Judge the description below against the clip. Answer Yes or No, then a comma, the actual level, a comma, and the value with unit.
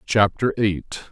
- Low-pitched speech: Yes, low, 105 Hz